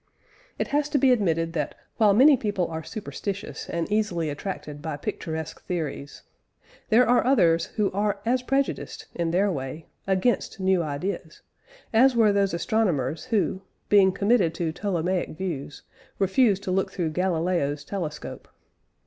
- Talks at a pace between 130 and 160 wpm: Yes, average, 145 wpm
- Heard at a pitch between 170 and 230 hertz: Yes, high, 190 Hz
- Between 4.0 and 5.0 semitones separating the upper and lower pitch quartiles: Yes, average, 4.6 semitones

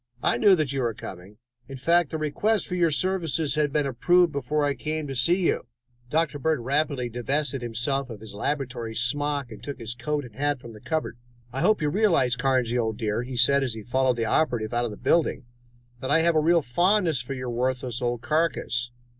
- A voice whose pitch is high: No, low, 135 Hz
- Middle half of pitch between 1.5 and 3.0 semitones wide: No, average, 4.3 semitones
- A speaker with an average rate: No, fast, 220 wpm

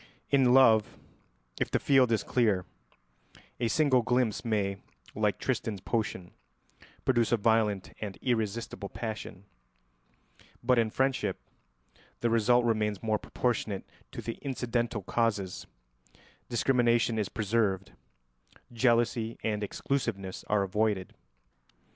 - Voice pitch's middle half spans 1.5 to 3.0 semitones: Yes, narrow, 2.6 semitones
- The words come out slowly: Yes, slow, 110 wpm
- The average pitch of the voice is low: Yes, low, 115 Hz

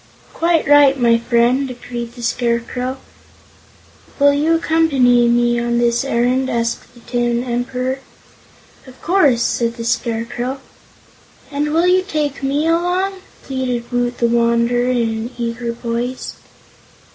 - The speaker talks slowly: Yes, slow, 130 wpm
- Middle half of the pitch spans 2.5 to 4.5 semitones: Yes, average, 3.0 semitones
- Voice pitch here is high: Yes, high, 245 Hz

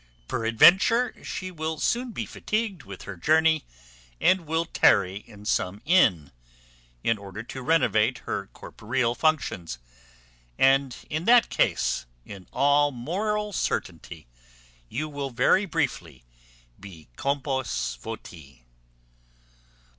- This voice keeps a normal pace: No, slow, 110 wpm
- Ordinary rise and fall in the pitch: No, wide, 8.6 semitones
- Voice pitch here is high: No, low, 135 Hz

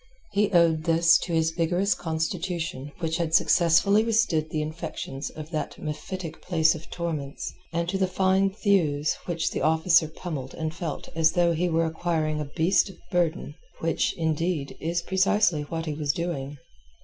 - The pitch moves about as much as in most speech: No, narrow, 2.1 semitones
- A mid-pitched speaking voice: Yes, medium, 165 Hz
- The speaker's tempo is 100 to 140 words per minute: No, average, 160 wpm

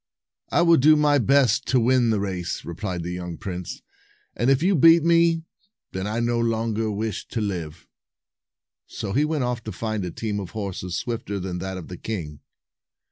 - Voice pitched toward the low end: Yes, low, 110 Hz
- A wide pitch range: Yes, wide, 5.9 semitones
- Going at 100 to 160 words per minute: No, average, 190 wpm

